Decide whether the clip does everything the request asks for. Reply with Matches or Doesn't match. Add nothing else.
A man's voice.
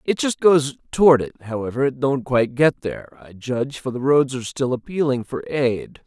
Matches